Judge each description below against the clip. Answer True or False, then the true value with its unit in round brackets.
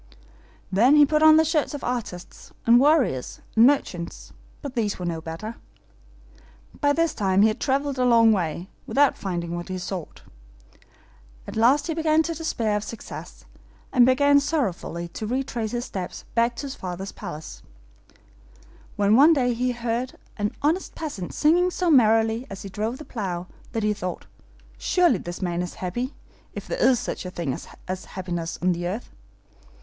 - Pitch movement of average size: False (7.3 semitones)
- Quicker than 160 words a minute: True (170 wpm)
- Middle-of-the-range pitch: False (230 Hz)